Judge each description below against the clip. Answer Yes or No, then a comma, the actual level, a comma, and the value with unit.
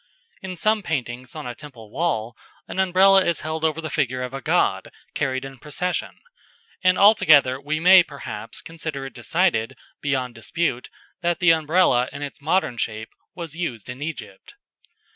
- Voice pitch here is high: No, medium, 150 Hz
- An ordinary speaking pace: Yes, average, 160 wpm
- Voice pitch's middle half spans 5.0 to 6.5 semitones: Yes, average, 5.3 semitones